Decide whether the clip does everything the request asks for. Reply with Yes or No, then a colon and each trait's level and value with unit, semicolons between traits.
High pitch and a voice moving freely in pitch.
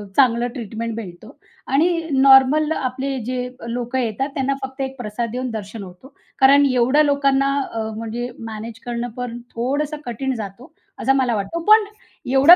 No: very high, 255 Hz; average, 3.0 semitones